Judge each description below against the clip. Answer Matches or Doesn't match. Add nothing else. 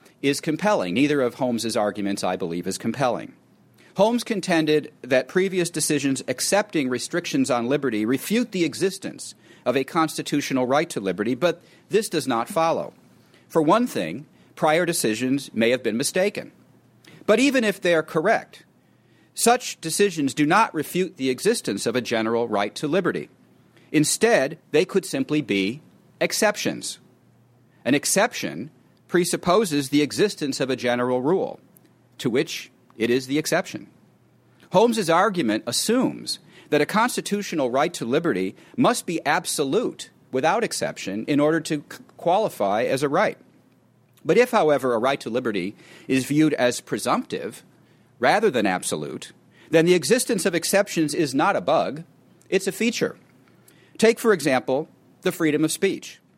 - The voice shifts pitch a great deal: Matches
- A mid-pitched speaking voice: Matches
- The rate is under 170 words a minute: Matches